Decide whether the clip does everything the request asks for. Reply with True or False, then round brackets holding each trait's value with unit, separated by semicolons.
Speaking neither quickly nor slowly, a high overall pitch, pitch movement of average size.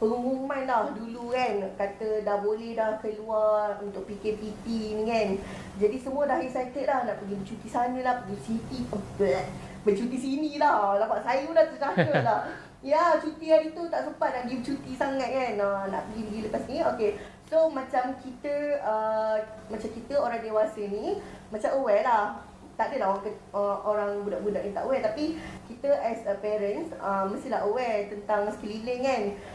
False (175 wpm; 225 Hz; 4.4 semitones)